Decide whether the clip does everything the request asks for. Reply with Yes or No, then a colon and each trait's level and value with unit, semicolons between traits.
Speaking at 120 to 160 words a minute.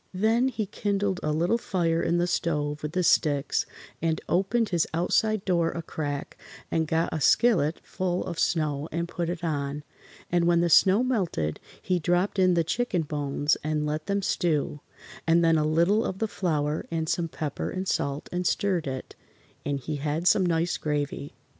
No: average, 185 wpm